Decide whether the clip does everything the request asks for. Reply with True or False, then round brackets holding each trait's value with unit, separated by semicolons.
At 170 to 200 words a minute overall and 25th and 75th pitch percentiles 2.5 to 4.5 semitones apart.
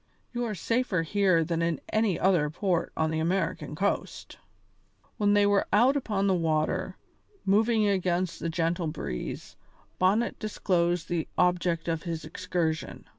False (145 wpm; 3.7 semitones)